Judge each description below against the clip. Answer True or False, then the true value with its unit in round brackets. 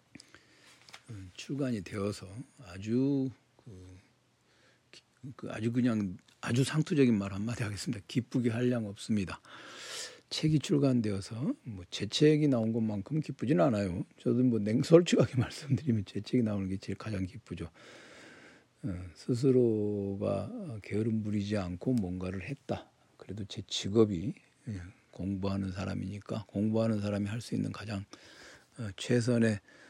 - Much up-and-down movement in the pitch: False (4.0 semitones)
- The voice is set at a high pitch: False (110 Hz)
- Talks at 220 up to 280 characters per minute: True (275 characters per minute)